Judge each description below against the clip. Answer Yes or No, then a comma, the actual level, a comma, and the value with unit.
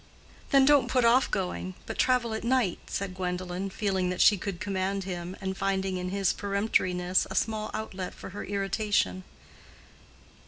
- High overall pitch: Yes, high, 195 Hz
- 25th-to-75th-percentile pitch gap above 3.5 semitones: No, average, 2.9 semitones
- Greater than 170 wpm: No, average, 160 wpm